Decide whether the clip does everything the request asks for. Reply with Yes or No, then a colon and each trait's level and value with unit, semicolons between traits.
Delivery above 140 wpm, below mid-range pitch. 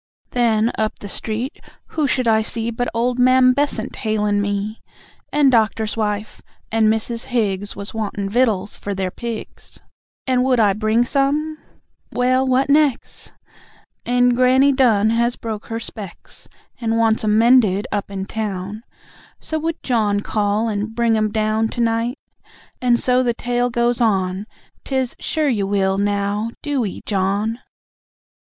No: average, 150 wpm; high, 225 Hz